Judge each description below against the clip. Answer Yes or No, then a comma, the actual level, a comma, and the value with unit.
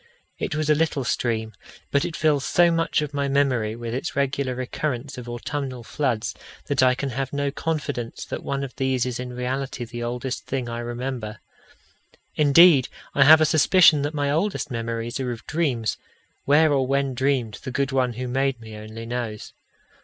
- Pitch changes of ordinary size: Yes, average, 3.0 semitones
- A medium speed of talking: Yes, average, 185 wpm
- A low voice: Yes, low, 130 Hz